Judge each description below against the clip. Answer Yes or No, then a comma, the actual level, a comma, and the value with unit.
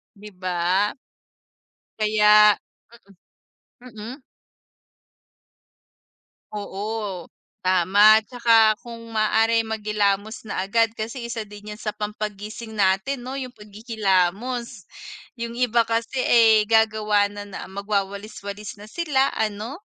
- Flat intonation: Yes, narrow, 2.1 semitones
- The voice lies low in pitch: No, high, 215 Hz